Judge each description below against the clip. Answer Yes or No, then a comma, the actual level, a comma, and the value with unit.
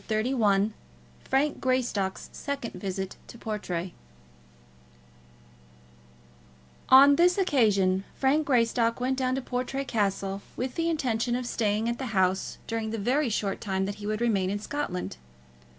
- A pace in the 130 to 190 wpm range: Yes, average, 140 wpm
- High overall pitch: Yes, high, 230 Hz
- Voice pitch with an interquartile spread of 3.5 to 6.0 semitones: Yes, average, 4.8 semitones